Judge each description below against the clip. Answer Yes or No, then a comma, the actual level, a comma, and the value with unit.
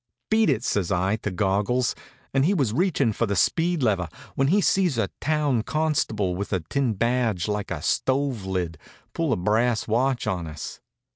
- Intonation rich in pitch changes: Yes, wide, 6.0 semitones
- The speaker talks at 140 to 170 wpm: No, average, 185 wpm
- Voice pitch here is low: Yes, low, 115 Hz